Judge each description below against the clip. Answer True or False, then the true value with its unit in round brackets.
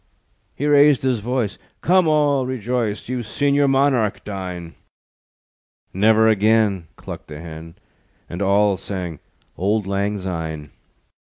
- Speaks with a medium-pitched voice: False (105 Hz)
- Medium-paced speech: False (120 wpm)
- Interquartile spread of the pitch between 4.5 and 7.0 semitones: True (5.6 semitones)